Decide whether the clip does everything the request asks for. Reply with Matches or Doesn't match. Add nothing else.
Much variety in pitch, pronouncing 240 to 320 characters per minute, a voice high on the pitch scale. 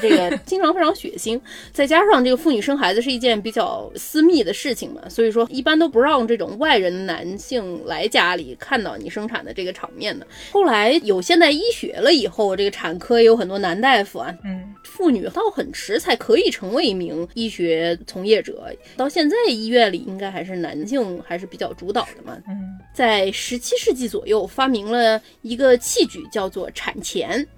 Matches